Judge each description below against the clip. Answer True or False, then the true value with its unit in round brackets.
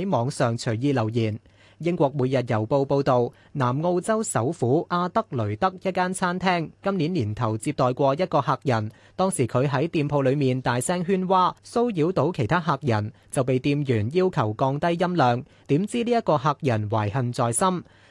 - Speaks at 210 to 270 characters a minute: True (255 characters per minute)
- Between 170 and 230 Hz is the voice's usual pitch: False (140 Hz)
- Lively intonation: True (6.5 semitones)